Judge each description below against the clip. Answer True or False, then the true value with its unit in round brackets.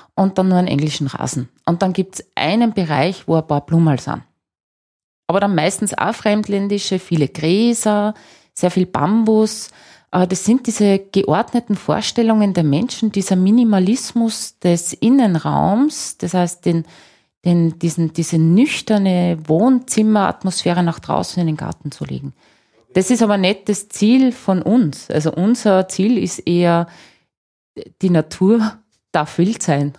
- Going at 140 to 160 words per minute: True (145 wpm)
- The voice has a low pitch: False (190 Hz)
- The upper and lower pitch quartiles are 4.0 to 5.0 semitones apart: True (4.5 semitones)